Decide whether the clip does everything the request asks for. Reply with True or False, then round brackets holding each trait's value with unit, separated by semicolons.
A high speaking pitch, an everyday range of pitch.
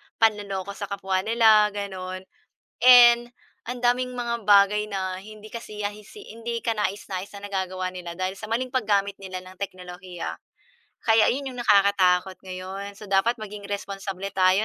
True (200 Hz; 3.0 semitones)